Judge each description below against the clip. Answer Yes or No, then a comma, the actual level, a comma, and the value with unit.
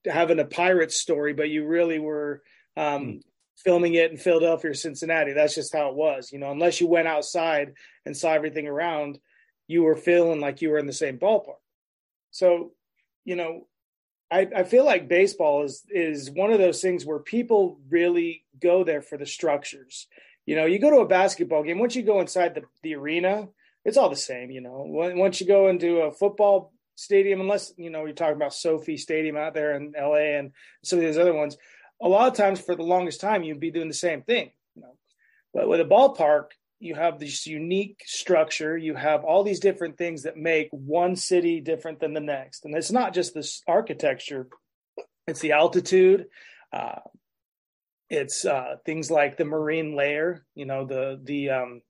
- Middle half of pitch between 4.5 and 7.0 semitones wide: No, average, 3.2 semitones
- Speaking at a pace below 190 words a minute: No, average, 195 wpm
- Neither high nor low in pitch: Yes, medium, 165 Hz